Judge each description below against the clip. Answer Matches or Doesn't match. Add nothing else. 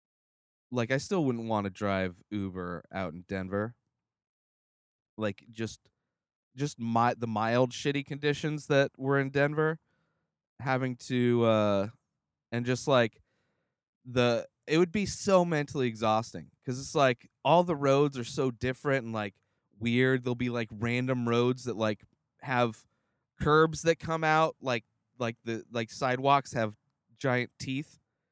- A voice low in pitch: Matches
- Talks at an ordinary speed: Matches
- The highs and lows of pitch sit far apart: Doesn't match